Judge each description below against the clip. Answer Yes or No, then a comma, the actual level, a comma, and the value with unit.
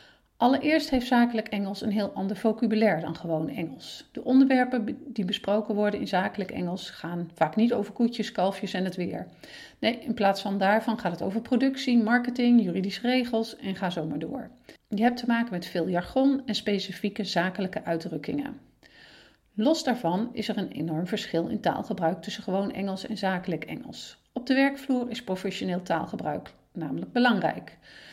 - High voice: Yes, high, 215 Hz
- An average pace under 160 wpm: No, average, 170 wpm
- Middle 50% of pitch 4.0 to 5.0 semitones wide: Yes, average, 4.4 semitones